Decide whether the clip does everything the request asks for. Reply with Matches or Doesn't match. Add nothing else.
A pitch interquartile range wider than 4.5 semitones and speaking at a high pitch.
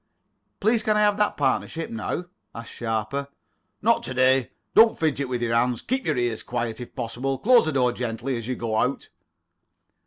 Doesn't match